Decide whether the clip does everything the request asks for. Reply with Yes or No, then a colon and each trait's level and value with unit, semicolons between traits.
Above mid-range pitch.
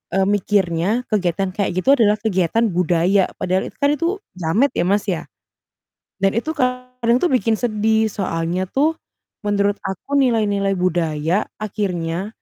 Yes: high, 200 Hz